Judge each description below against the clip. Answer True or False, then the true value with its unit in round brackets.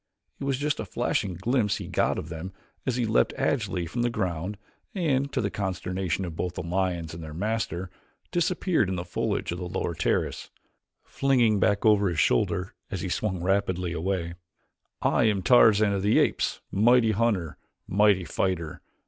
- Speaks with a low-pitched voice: True (95 Hz)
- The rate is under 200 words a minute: True (175 wpm)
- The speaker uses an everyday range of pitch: True (4.2 semitones)